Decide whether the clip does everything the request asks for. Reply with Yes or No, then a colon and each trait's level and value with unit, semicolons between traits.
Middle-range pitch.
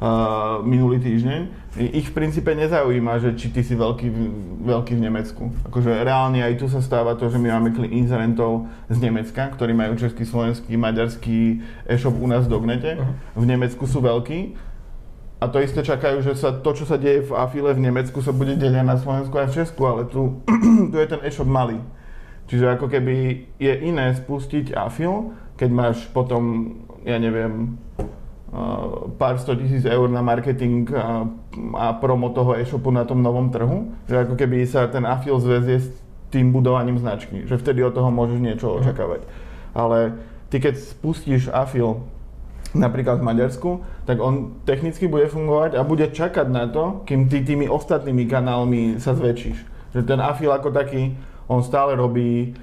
No: low, 125 Hz